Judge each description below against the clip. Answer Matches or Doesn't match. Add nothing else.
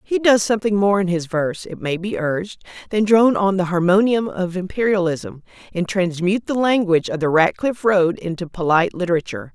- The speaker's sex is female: Matches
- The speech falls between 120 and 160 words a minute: Doesn't match